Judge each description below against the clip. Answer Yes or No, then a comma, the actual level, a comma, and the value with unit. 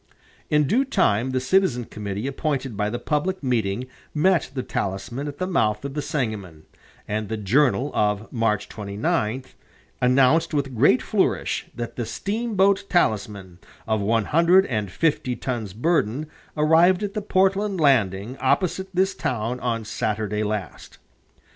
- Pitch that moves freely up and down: Yes, wide, 7.2 semitones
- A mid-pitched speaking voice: No, low, 125 Hz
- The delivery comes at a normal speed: Yes, average, 145 wpm